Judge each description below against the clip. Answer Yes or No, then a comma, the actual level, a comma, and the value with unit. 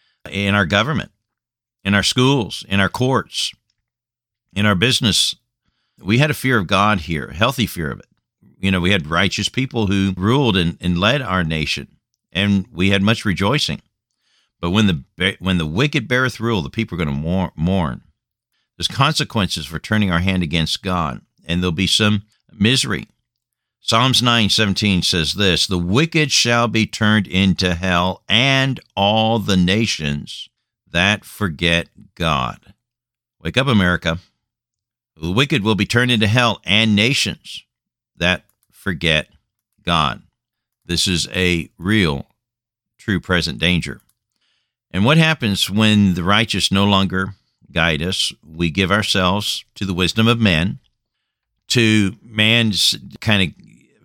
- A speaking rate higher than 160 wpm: No, average, 145 wpm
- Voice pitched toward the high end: No, low, 100 Hz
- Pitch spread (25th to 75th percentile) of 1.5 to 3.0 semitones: No, average, 4.1 semitones